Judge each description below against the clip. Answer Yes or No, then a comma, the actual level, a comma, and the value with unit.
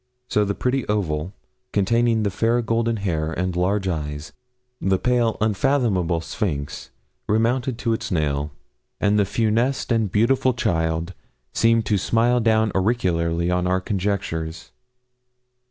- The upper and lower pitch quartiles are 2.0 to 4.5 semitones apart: No, average, 4.9 semitones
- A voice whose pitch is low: Yes, low, 100 Hz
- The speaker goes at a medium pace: No, slow, 130 wpm